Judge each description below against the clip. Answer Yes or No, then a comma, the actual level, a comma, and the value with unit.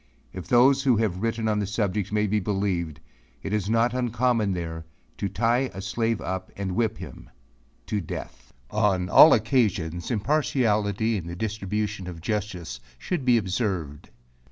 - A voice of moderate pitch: No, low, 105 Hz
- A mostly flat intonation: No, average, 3.6 semitones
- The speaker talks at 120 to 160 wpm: Yes, average, 155 wpm